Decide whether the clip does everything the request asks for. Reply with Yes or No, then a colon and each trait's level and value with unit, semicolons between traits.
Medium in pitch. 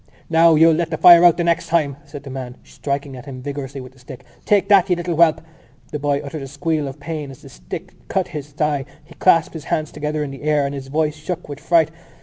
Yes: medium, 150 Hz